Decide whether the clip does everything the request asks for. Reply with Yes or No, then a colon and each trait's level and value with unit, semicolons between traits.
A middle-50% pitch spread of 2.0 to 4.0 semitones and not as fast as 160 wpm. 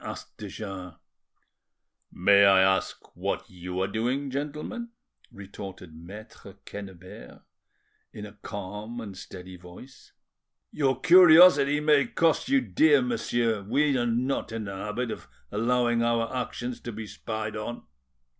No: average, 5.1 semitones; slow, 135 wpm